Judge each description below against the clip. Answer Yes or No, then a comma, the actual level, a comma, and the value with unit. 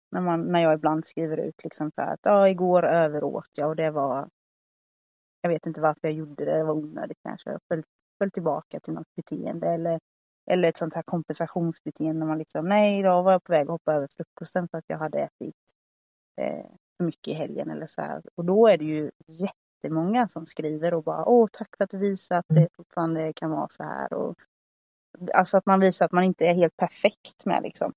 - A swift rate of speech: Yes, fast, 220 wpm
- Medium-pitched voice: Yes, medium, 165 Hz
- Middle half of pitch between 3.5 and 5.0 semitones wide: No, narrow, 2.5 semitones